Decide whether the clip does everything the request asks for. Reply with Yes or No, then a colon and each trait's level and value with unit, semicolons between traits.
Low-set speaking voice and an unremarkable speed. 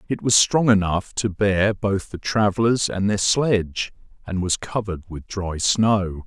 Yes: low, 100 Hz; average, 170 wpm